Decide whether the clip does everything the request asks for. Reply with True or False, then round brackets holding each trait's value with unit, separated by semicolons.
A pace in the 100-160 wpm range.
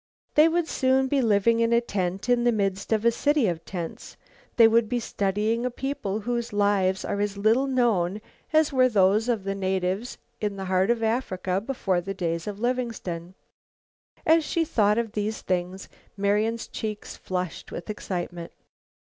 False (170 wpm)